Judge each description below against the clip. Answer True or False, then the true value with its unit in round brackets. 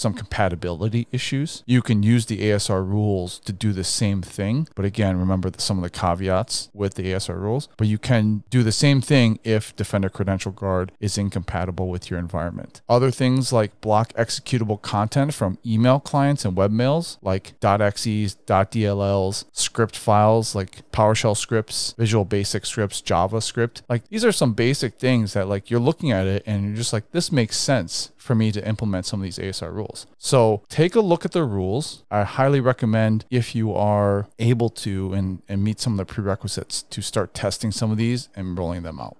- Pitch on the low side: True (110 Hz)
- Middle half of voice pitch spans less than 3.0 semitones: False (3.5 semitones)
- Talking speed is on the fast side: False (190 wpm)